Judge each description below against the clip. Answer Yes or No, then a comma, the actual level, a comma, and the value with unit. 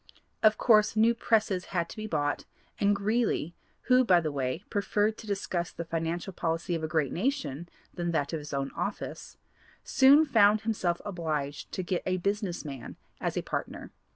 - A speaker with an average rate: Yes, average, 180 wpm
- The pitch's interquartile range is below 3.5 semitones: No, average, 4.8 semitones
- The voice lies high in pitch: No, medium, 180 Hz